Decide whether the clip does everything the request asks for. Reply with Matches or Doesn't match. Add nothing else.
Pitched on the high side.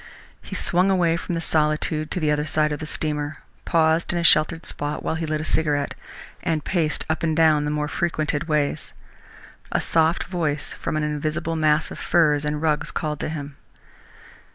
Doesn't match